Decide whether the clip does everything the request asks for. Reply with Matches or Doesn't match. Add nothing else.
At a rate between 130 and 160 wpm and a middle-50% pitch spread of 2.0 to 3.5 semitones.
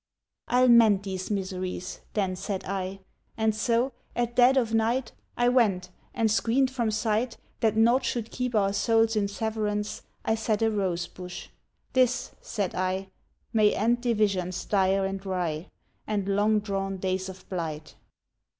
Matches